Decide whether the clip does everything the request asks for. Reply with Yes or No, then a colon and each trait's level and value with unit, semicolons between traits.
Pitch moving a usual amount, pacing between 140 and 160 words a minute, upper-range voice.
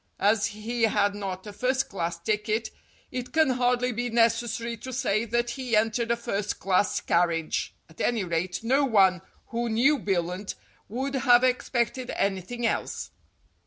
Yes: average, 3.6 semitones; average, 155 wpm; high, 225 Hz